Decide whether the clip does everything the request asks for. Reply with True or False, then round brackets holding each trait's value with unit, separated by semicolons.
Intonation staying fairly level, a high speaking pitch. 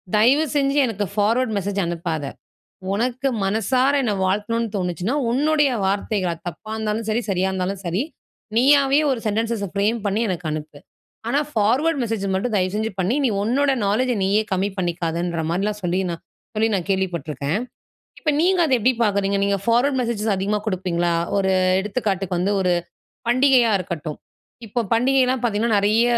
False (4.3 semitones; 210 Hz)